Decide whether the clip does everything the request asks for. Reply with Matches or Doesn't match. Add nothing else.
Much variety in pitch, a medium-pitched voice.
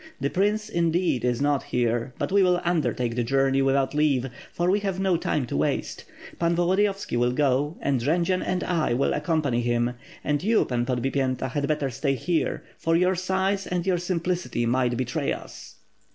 Matches